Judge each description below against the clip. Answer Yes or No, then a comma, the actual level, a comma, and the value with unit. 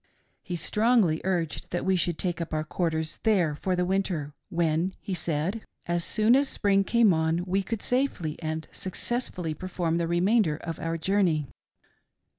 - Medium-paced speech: Yes, average, 165 wpm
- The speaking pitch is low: No, medium, 175 Hz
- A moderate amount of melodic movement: Yes, average, 3.4 semitones